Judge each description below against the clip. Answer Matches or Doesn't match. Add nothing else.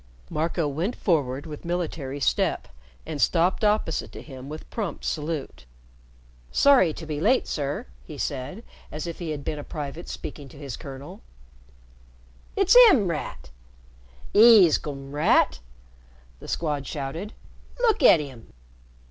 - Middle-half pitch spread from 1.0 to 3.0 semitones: Doesn't match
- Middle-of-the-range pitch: Matches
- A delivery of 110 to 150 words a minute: Matches